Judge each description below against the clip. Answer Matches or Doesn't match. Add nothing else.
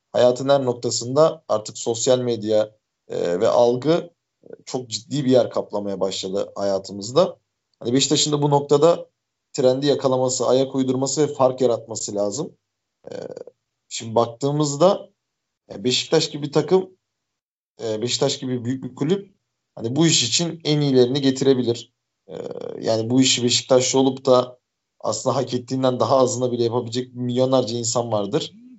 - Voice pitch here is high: Doesn't match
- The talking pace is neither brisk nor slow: Matches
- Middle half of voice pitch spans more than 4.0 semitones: Doesn't match